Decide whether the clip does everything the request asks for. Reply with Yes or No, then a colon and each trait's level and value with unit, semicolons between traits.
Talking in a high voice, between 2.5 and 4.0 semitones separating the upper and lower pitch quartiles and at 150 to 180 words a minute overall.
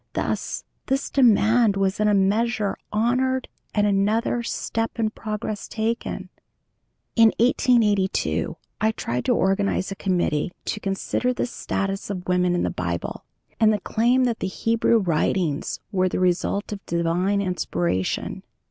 No: high, 205 Hz; average, 3.5 semitones; average, 140 wpm